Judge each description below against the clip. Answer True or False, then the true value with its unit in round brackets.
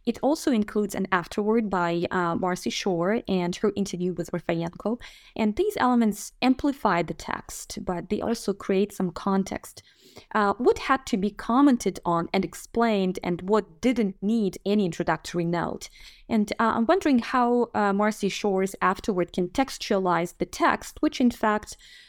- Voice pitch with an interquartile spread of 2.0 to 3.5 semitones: False (4.1 semitones)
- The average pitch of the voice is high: True (205 Hz)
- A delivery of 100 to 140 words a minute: False (155 wpm)